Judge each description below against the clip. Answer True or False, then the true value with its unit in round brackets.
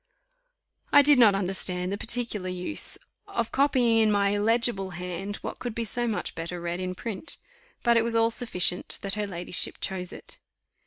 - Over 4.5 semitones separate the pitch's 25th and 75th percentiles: False (4.2 semitones)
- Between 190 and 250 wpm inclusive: False (175 wpm)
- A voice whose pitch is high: True (205 Hz)